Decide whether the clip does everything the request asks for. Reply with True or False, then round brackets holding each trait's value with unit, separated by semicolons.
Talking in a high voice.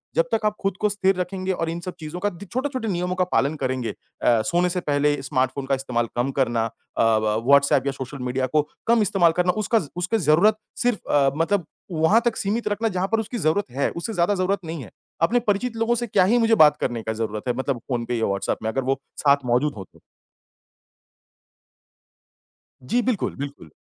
False (165 Hz)